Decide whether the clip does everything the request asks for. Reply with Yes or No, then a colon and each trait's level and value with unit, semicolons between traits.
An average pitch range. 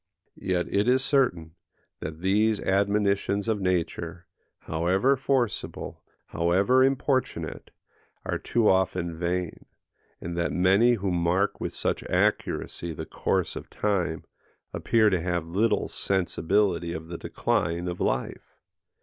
Yes: average, 3.6 semitones